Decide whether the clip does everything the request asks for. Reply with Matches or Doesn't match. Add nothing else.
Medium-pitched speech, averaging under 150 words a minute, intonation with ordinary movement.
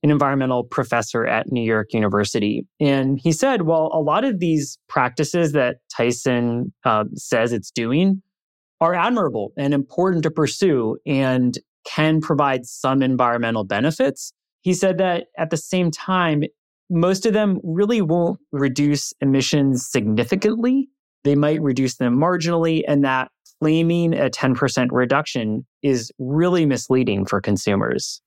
Matches